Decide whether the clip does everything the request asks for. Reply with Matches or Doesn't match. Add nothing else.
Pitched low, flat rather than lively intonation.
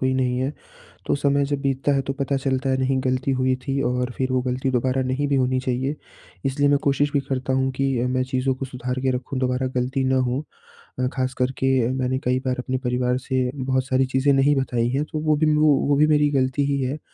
Matches